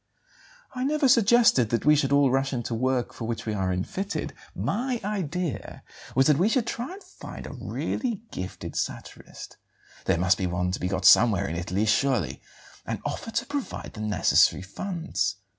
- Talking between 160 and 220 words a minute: Yes, average, 175 wpm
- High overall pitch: No, low, 135 Hz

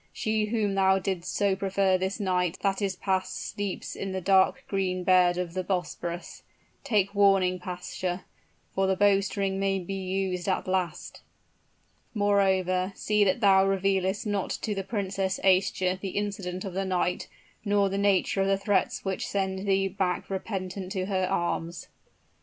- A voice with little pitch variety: Yes, narrow, 1.2 semitones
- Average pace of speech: Yes, average, 160 wpm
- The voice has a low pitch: No, high, 190 Hz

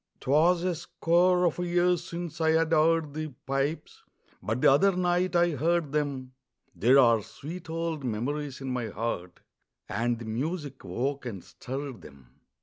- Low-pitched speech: No, medium, 150 Hz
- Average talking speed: Yes, average, 150 wpm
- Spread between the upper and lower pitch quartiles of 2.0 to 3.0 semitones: No, average, 5.1 semitones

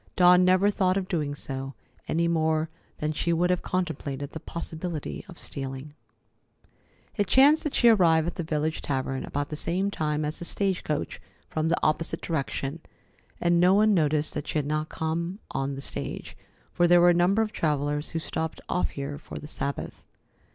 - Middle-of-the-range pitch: Yes, medium, 160 Hz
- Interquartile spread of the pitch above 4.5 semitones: No, average, 3.2 semitones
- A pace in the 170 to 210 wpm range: Yes, average, 185 wpm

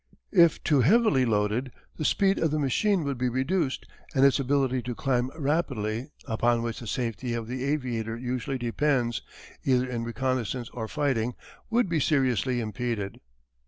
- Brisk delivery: No, average, 160 wpm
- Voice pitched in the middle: No, low, 130 Hz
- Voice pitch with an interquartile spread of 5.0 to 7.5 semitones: No, average, 3.2 semitones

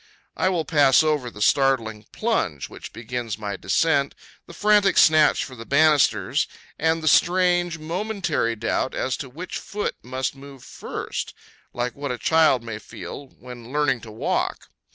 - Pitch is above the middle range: No, medium, 140 Hz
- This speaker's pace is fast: No, average, 155 wpm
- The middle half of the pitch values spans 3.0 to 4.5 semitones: No, average, 5.1 semitones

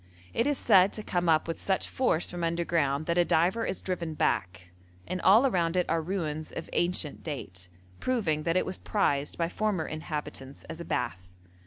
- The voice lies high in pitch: No, medium, 170 Hz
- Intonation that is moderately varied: Yes, average, 3.3 semitones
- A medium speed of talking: Yes, average, 190 wpm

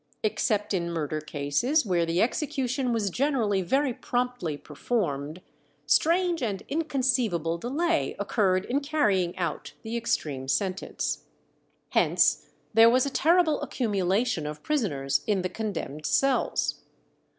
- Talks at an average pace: No, slow, 120 wpm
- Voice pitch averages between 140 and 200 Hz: No, high, 215 Hz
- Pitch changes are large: Yes, wide, 7.6 semitones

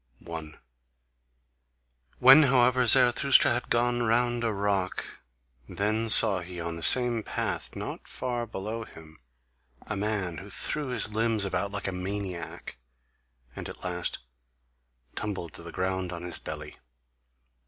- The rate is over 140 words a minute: No, slow, 135 wpm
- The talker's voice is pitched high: No, low, 105 Hz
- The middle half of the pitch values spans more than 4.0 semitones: Yes, average, 4.9 semitones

